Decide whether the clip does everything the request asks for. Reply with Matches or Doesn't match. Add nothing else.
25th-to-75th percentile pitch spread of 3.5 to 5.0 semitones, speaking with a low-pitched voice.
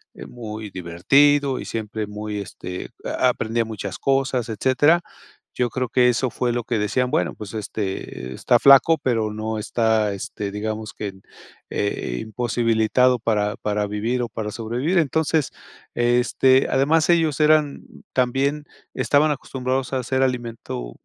Matches